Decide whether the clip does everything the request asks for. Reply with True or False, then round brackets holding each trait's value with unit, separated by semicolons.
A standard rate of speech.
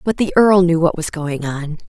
False (250 wpm)